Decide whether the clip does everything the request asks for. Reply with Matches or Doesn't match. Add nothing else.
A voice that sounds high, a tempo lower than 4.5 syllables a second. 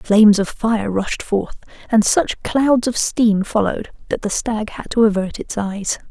Matches